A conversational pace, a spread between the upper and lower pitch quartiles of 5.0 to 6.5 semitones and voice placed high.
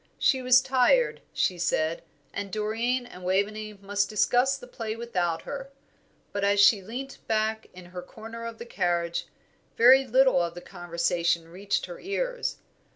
Yes: average, 160 wpm; wide, 5.5 semitones; high, 215 Hz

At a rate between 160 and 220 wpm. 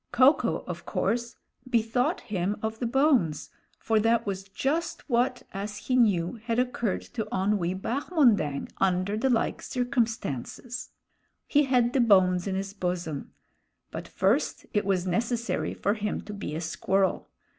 No: average, 150 wpm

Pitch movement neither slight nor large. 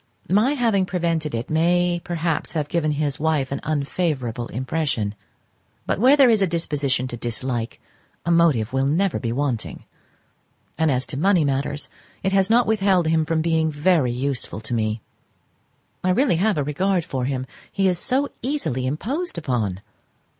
No: wide, 5.7 semitones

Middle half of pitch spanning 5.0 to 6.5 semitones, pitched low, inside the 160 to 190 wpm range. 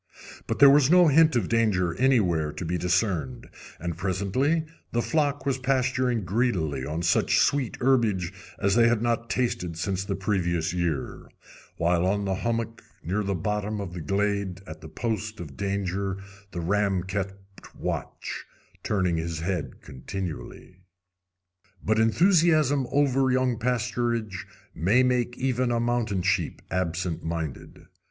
No: wide, 5.5 semitones; low, 100 Hz; average, 145 wpm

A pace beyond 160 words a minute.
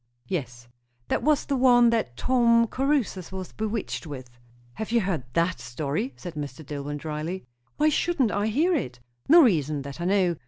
Yes: average, 170 wpm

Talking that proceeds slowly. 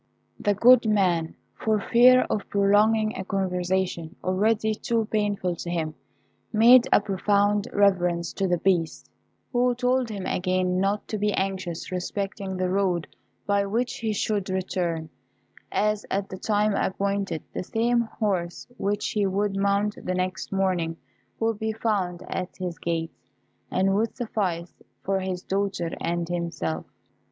No: average, 145 wpm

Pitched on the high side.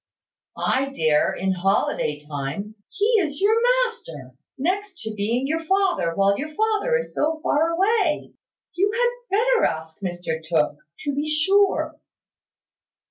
Yes: very high, 295 Hz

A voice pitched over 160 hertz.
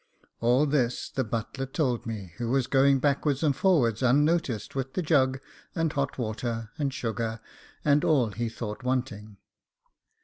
No: low, 130 Hz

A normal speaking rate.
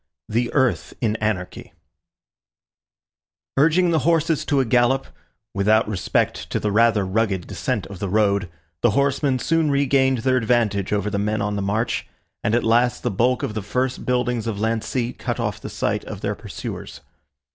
Yes: average, 170 wpm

